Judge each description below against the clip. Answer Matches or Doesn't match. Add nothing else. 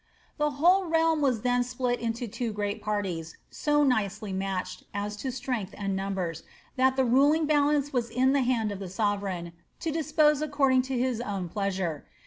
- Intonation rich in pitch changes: Matches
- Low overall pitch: Doesn't match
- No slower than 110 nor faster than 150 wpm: Doesn't match